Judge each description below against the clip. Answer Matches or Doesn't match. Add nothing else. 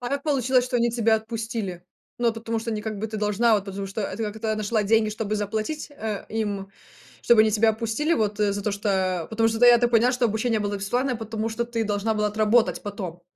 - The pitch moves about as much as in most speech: Doesn't match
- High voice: Matches